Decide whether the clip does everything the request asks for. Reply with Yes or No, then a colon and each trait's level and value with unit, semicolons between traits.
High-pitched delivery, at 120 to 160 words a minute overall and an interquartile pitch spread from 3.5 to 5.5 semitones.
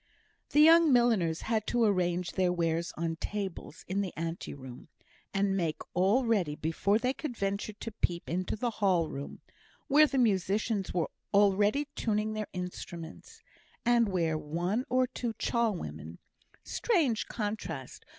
Yes: high, 200 Hz; average, 150 wpm; average, 5.1 semitones